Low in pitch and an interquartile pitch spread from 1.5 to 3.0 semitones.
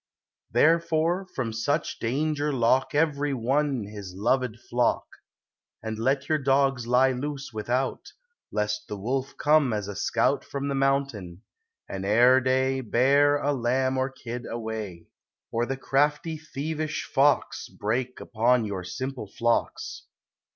No: low, 130 Hz; average, 3.7 semitones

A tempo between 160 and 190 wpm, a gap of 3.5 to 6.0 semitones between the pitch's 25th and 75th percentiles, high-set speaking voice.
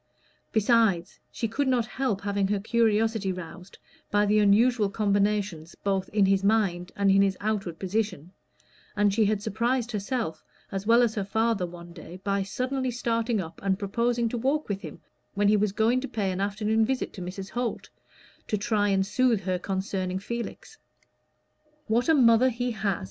No: average, 175 wpm; average, 3.1 semitones; high, 210 Hz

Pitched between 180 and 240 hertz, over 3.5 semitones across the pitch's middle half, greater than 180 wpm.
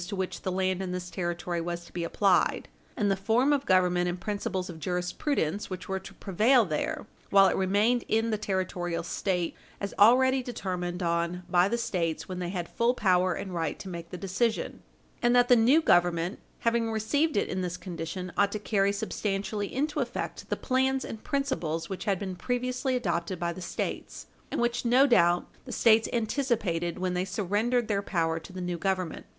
Yes: high, 190 Hz; average, 4.5 semitones; average, 195 wpm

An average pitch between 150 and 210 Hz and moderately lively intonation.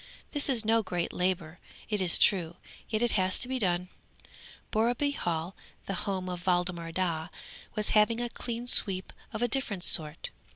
Yes: high, 190 Hz; average, 4.4 semitones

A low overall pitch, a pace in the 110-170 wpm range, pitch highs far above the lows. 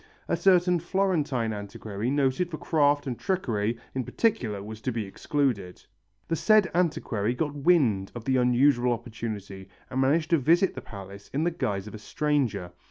Yes: low, 130 Hz; average, 165 wpm; wide, 6.7 semitones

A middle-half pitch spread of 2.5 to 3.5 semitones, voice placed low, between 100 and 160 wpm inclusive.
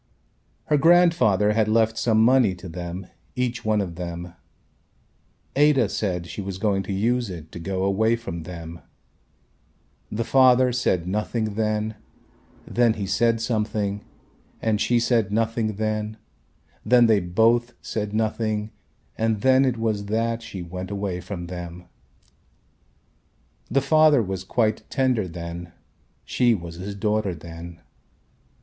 No: average, 3.9 semitones; low, 105 Hz; slow, 135 wpm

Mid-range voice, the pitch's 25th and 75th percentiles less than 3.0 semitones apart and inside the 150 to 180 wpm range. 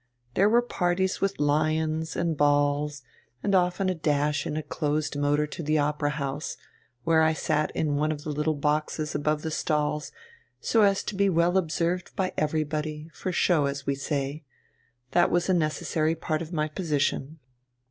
Yes: medium, 155 Hz; narrow, 2.4 semitones; average, 175 wpm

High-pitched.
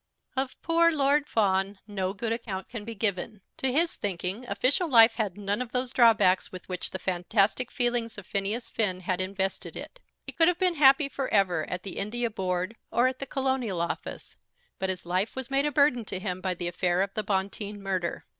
Yes: high, 210 Hz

